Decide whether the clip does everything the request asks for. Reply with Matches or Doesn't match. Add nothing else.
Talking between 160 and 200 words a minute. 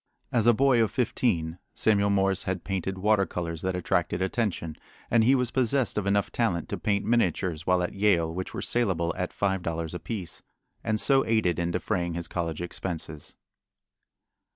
Matches